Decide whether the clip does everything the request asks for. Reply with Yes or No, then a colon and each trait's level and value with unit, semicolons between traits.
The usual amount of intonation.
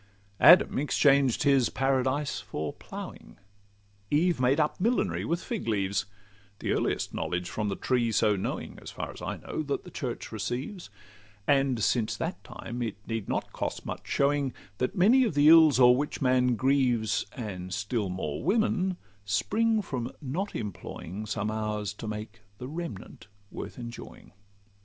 No: wide, 5.7 semitones